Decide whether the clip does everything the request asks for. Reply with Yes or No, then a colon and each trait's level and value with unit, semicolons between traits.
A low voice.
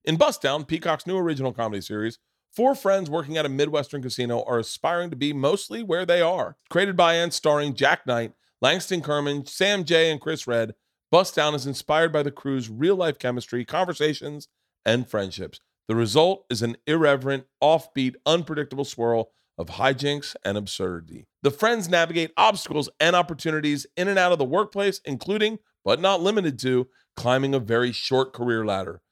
No: medium, 145 Hz